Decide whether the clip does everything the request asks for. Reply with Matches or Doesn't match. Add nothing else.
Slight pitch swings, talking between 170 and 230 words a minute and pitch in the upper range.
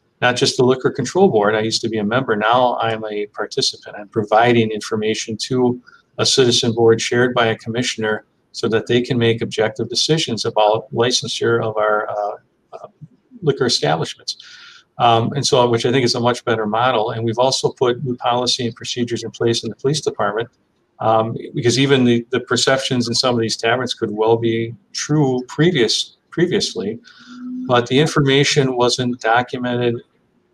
Doesn't match